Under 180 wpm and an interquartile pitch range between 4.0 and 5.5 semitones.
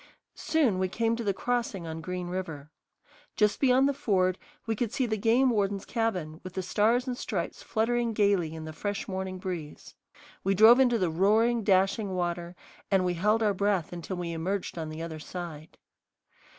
No: average, 185 wpm; average, 4.4 semitones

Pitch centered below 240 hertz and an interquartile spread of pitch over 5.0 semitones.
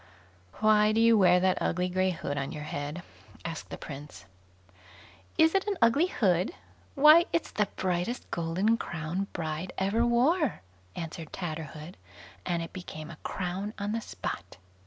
Yes: medium, 185 Hz; wide, 5.6 semitones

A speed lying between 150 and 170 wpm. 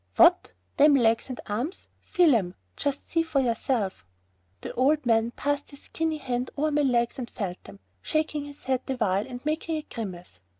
No: average, 185 wpm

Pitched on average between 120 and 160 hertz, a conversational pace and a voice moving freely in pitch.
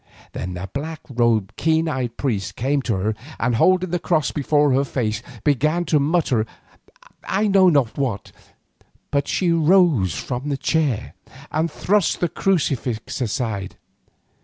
Yes: medium, 140 Hz; average, 145 wpm; wide, 5.9 semitones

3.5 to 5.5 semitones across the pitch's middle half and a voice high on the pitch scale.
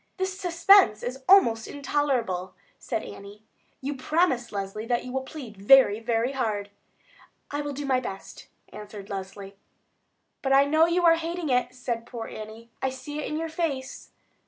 Yes: average, 5.2 semitones; very high, 255 Hz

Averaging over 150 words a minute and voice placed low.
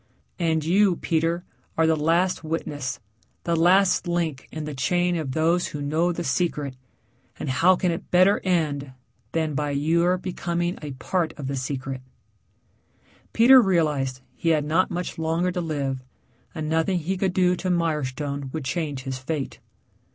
No: average, 165 wpm; medium, 160 Hz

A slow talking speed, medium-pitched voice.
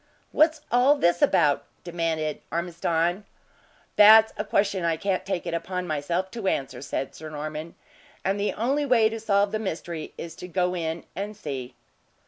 No: average, 165 wpm; medium, 180 Hz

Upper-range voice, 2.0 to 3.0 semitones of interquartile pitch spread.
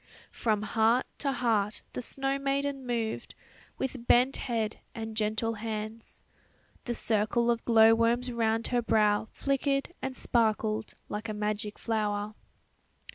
Yes: high, 225 Hz; narrow, 2.4 semitones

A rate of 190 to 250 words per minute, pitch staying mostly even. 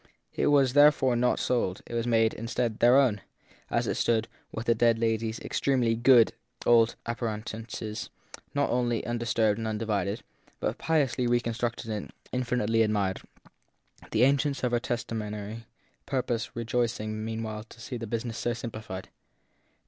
No: average, 150 wpm; narrow, 1.8 semitones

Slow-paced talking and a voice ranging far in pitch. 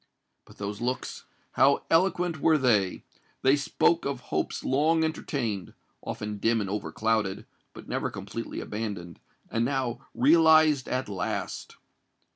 Yes: slow, 105 wpm; wide, 6.6 semitones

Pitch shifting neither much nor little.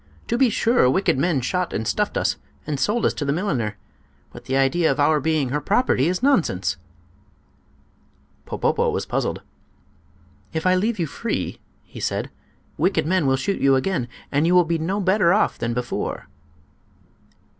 No: wide, 5.9 semitones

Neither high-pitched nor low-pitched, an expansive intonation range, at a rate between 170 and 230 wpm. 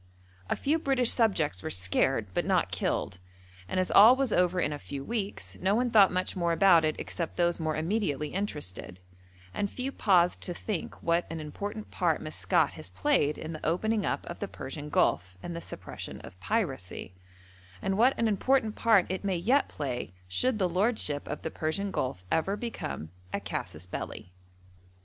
Yes: medium, 180 Hz; wide, 6.3 semitones; average, 180 wpm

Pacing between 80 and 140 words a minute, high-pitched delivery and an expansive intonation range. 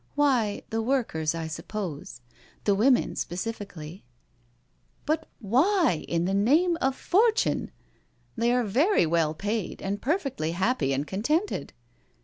Yes: slow, 135 wpm; high, 215 Hz; wide, 8.3 semitones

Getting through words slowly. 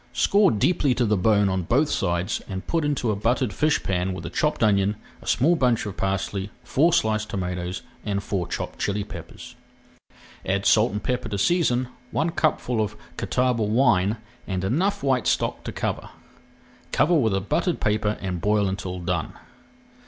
No: average, 175 wpm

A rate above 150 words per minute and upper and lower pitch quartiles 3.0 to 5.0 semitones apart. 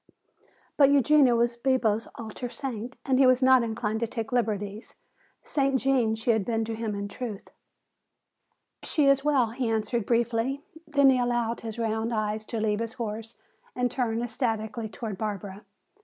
No: average, 165 wpm; narrow, 2.6 semitones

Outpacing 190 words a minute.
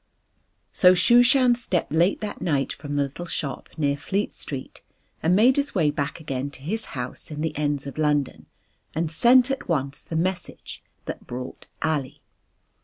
No: average, 170 wpm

